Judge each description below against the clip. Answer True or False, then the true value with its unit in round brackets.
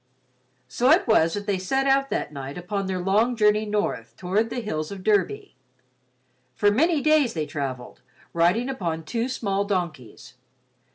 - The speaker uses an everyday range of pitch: False (5.9 semitones)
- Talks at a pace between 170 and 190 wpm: False (160 wpm)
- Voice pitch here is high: True (205 Hz)